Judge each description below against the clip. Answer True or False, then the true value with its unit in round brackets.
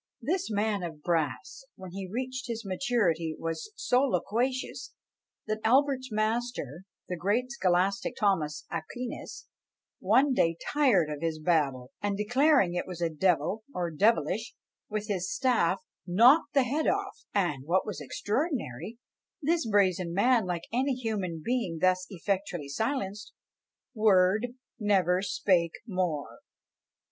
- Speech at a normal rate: False (130 wpm)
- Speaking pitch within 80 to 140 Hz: False (200 Hz)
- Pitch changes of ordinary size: False (5.9 semitones)